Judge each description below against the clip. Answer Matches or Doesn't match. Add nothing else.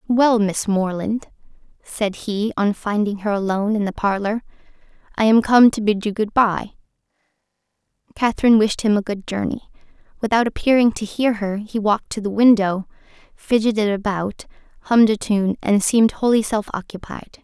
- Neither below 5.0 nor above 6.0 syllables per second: Matches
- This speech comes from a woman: Matches